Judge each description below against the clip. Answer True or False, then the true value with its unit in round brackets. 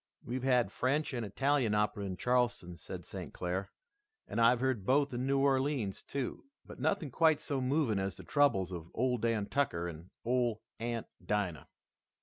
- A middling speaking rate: True (170 wpm)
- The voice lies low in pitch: True (120 Hz)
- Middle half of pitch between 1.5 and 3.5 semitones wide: False (5.2 semitones)